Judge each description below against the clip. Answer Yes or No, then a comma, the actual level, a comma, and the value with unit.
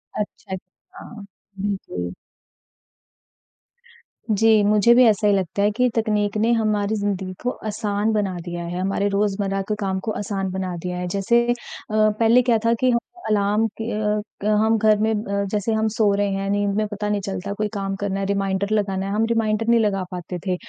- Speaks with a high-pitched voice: Yes, high, 205 Hz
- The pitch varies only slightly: Yes, narrow, 1.8 semitones